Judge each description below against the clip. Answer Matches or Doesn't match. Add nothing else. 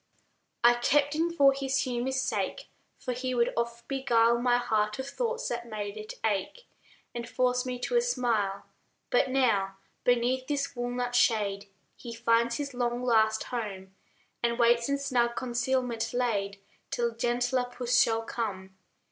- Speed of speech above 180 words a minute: Doesn't match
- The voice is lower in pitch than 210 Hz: Doesn't match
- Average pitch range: Doesn't match